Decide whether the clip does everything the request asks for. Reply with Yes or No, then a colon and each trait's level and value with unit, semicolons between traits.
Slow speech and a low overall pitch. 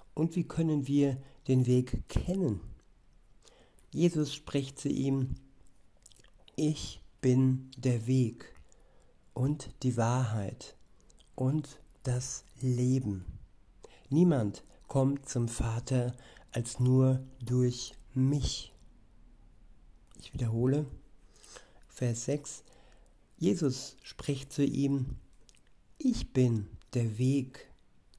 Yes: slow, 85 wpm; low, 130 Hz